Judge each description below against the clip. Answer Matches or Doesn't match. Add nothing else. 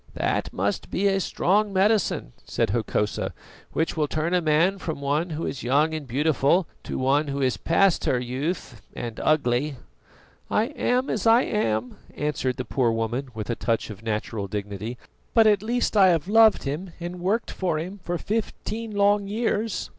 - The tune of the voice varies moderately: Doesn't match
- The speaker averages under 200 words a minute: Matches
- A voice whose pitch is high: Doesn't match